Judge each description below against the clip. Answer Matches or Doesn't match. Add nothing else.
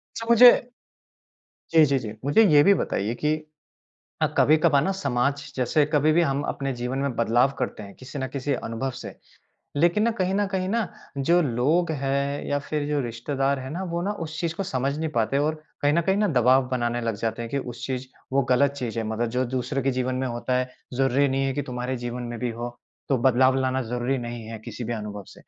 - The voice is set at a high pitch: Doesn't match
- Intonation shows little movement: Doesn't match